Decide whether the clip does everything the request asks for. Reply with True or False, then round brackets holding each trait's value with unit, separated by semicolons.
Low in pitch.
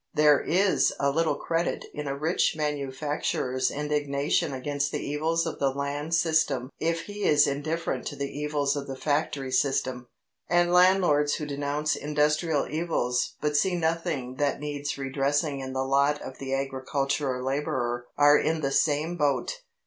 False (145 Hz)